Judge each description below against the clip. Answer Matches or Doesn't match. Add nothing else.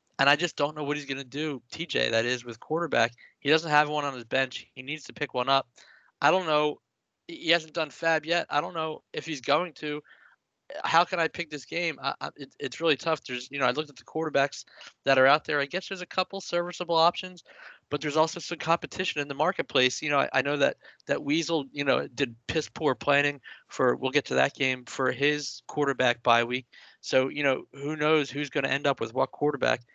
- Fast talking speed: Matches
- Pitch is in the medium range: Matches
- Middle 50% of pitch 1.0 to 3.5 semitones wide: Matches